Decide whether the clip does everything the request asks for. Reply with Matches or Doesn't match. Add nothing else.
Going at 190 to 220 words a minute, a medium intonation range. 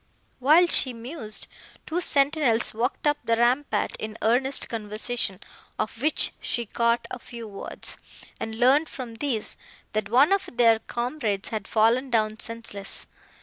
Doesn't match